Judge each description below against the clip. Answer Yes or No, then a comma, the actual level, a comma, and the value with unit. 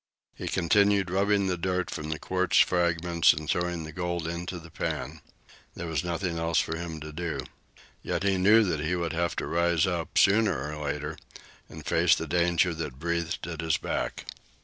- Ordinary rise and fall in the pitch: No, narrow, 1.9 semitones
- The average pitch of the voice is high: No, very low, 85 Hz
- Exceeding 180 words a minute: Yes, average, 190 wpm